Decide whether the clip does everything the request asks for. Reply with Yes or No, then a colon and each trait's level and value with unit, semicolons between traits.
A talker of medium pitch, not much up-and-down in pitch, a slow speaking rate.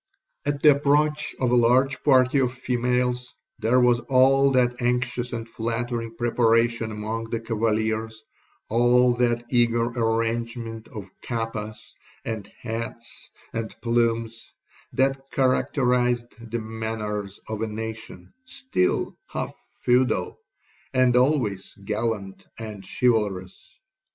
No: low, 115 Hz; narrow, 1.9 semitones; slow, 105 wpm